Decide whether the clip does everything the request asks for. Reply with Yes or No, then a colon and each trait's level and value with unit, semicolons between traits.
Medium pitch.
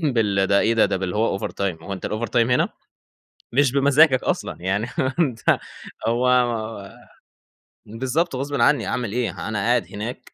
No: low, 115 Hz